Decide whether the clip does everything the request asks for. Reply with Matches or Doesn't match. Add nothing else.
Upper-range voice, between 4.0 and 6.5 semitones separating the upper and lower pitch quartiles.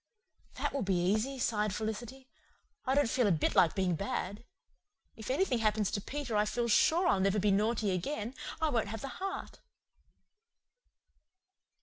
Matches